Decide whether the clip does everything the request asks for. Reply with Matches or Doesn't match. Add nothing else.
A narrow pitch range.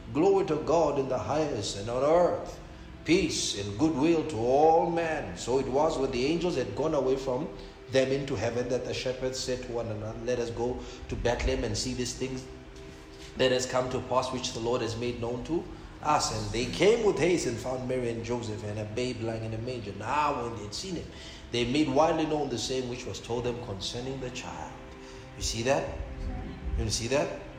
Doesn't match